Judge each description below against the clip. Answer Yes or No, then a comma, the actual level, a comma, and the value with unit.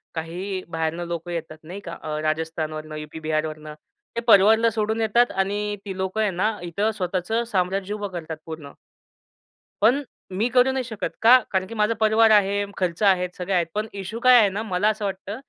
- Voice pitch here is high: Yes, high, 195 Hz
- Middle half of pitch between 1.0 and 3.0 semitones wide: No, average, 4.3 semitones